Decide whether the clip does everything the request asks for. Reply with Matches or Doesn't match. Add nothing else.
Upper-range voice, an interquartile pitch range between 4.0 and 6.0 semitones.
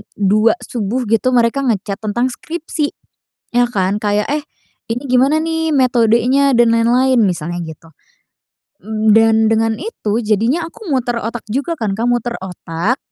Doesn't match